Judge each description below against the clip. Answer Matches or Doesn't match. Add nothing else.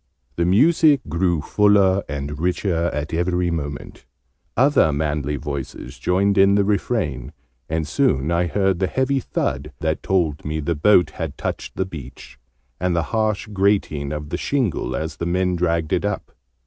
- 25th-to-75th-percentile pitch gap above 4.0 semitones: Matches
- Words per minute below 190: Matches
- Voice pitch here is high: Doesn't match